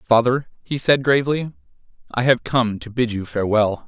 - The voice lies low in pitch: Yes, low, 120 Hz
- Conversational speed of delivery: Yes, average, 170 wpm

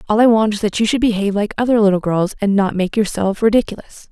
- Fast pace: Yes, fast, 250 wpm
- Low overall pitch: No, high, 210 Hz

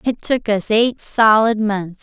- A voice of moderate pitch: No, high, 215 Hz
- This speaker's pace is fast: No, average, 180 wpm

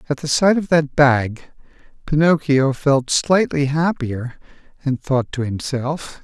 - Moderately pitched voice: Yes, medium, 145 Hz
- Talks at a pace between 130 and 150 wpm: Yes, slow, 135 wpm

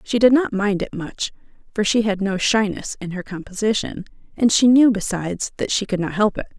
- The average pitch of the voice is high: Yes, high, 205 Hz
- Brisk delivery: Yes, fast, 220 wpm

